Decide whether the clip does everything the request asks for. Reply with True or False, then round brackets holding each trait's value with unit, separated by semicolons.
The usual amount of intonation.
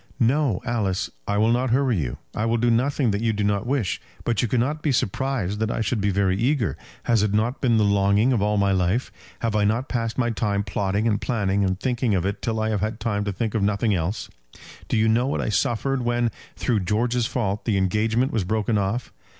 True (3.0 semitones)